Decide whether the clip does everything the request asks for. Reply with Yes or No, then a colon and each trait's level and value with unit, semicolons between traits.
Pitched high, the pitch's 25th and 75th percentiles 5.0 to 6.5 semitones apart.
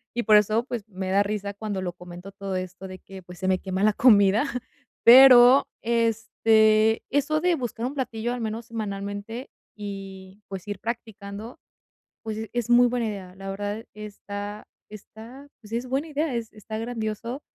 No: high, 215 Hz; average, 3.0 semitones